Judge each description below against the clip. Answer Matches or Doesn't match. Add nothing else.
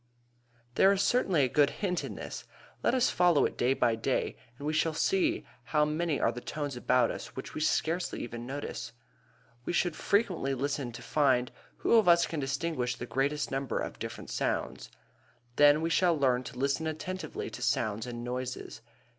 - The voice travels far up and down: Doesn't match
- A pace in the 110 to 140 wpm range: Doesn't match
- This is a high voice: Doesn't match